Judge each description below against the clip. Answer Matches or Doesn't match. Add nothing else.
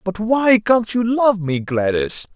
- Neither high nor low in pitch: Doesn't match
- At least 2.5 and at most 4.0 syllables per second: Matches